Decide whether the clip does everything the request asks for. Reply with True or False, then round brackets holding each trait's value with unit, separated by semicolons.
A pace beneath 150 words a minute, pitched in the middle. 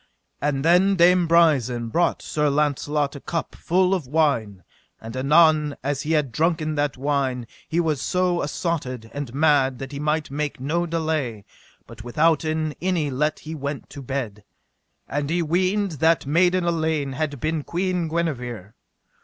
False (155 wpm; 150 Hz)